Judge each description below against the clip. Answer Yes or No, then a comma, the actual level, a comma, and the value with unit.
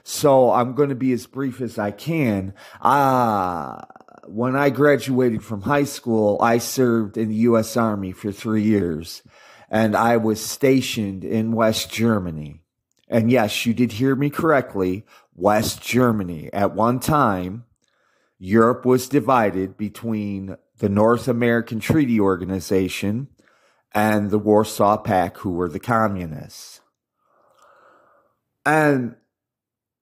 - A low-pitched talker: Yes, low, 110 Hz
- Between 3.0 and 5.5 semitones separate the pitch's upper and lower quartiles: Yes, average, 3.3 semitones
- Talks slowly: Yes, slow, 130 wpm